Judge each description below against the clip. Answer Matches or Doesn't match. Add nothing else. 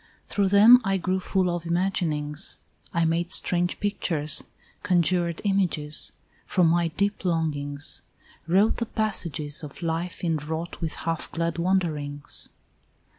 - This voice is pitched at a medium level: Matches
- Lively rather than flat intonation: Doesn't match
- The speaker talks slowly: Matches